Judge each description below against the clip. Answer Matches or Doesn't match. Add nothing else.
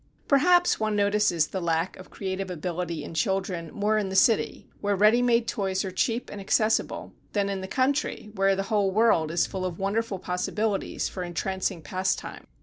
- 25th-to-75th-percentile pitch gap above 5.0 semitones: Doesn't match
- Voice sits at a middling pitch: Doesn't match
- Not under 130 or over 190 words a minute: Matches